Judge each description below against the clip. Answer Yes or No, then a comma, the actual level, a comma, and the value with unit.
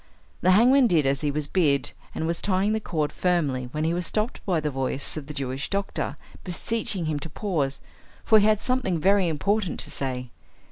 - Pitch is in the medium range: Yes, medium, 170 Hz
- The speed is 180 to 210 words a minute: Yes, average, 200 wpm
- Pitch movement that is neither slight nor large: No, wide, 5.8 semitones